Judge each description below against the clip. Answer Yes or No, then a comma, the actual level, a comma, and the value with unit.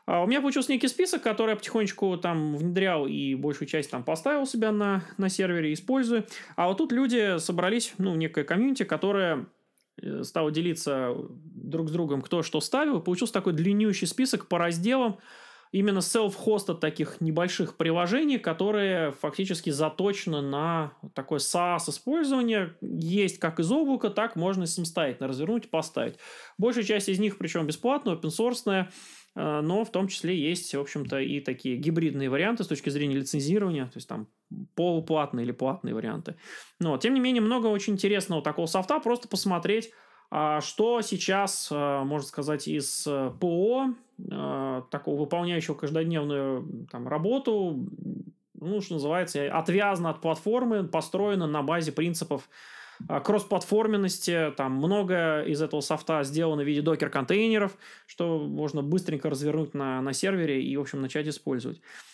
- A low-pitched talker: No, medium, 175 Hz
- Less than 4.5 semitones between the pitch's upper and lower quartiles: No, wide, 5.5 semitones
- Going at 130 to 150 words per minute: Yes, average, 145 wpm